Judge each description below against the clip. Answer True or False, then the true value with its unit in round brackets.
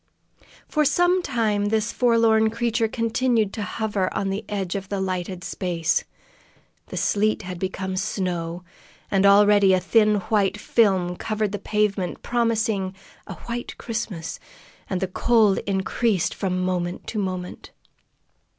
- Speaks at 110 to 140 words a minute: True (135 wpm)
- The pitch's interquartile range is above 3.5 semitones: False (3.1 semitones)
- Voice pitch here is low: False (205 Hz)